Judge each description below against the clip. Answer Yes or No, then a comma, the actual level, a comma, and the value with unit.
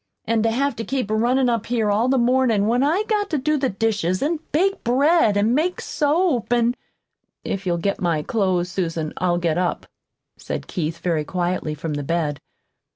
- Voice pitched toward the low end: No, high, 225 Hz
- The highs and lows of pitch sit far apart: Yes, wide, 7.1 semitones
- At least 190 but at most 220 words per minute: Yes, average, 195 wpm